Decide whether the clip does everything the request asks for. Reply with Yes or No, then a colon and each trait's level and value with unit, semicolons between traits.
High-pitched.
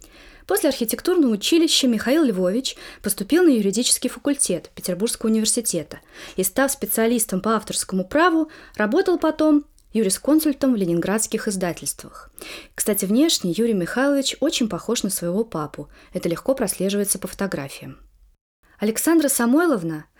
Yes: high, 225 Hz